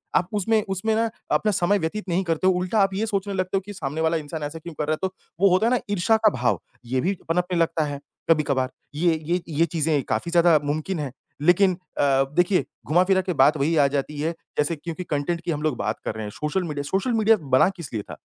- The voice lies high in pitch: No, medium, 170 Hz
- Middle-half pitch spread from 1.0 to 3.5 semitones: No, average, 4.2 semitones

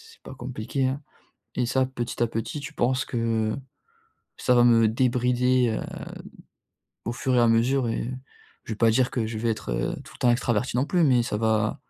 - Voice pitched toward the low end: Yes, low, 120 Hz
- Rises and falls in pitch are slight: Yes, narrow, 2.1 semitones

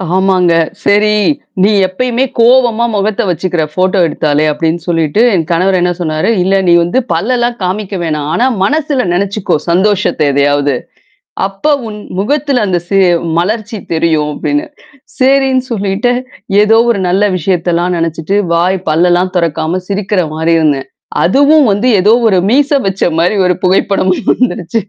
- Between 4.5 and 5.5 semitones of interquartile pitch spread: Yes, average, 4.9 semitones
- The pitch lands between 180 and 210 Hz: Yes, high, 190 Hz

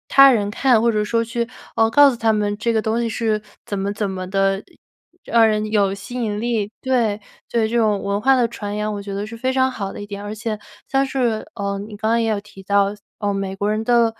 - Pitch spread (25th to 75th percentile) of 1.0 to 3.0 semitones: Yes, narrow, 2.4 semitones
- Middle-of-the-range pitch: No, high, 215 Hz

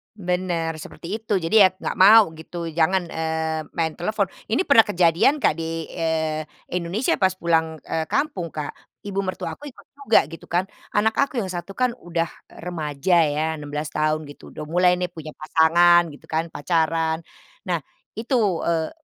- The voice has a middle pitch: Yes, medium, 170 Hz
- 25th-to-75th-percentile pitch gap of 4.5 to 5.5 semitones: No, average, 2.8 semitones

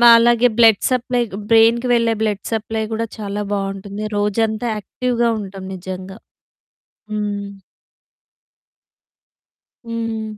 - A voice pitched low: No, high, 220 Hz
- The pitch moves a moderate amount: No, narrow, 2.3 semitones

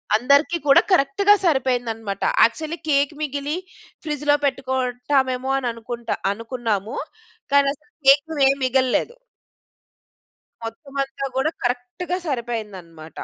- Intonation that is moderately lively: Yes, average, 3.2 semitones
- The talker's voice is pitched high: Yes, very high, 265 Hz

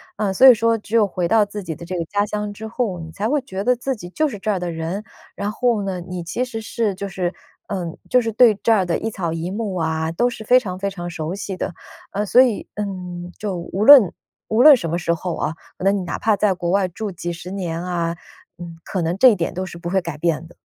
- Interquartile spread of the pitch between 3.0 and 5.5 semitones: Yes, average, 3.8 semitones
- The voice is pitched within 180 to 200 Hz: Yes, high, 195 Hz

